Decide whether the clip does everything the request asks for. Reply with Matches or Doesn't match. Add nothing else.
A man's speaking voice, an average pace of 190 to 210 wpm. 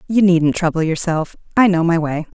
Doesn't match